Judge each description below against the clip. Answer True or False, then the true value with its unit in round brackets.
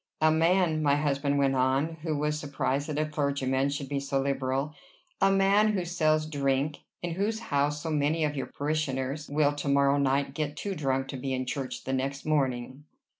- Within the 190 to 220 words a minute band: True (195 wpm)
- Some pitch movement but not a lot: False (2.1 semitones)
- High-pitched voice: False (145 Hz)